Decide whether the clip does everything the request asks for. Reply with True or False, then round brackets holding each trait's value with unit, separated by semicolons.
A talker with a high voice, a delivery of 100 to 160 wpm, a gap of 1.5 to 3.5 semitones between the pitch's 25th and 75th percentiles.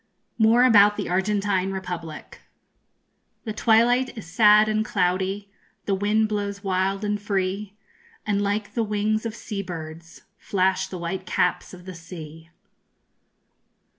True (200 Hz; 135 wpm; 2.4 semitones)